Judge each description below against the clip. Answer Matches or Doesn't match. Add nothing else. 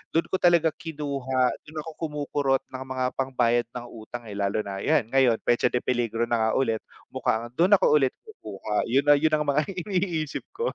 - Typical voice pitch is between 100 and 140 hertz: Matches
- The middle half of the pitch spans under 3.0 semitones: Doesn't match